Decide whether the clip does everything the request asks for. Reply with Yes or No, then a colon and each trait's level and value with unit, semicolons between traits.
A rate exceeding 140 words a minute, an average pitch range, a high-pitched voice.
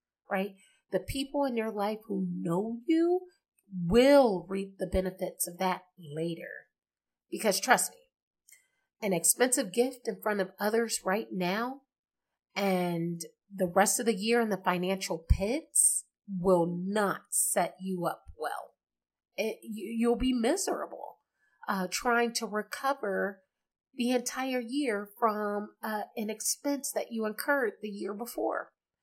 No: slow, 135 wpm; average, 4.6 semitones; high, 210 Hz